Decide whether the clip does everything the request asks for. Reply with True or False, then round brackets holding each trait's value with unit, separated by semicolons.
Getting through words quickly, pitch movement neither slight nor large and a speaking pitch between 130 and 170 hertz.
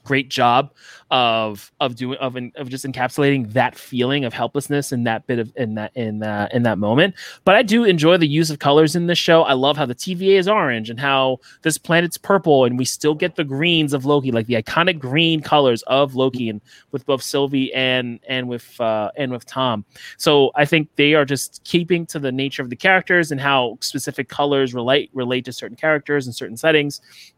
True (215 wpm; 3.6 semitones; 140 Hz)